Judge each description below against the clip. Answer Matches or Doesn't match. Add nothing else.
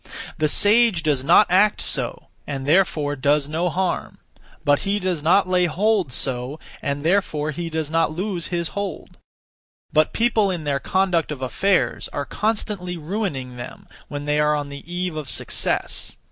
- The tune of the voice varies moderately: Matches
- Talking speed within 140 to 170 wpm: Matches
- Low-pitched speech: Doesn't match